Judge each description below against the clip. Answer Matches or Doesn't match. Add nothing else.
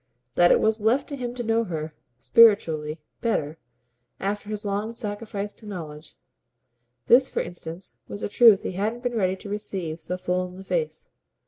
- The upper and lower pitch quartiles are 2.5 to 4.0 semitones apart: Doesn't match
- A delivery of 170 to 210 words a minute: Matches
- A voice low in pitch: Doesn't match